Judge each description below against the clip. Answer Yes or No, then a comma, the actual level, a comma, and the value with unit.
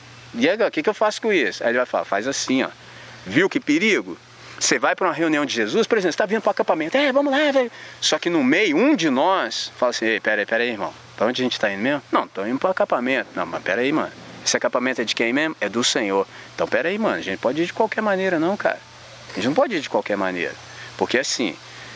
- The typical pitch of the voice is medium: No, high, 215 Hz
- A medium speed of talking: No, fast, 255 wpm